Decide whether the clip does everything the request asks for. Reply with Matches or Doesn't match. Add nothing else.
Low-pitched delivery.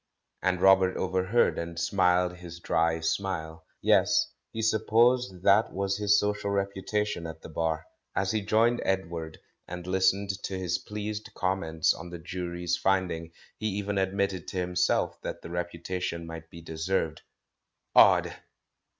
Matches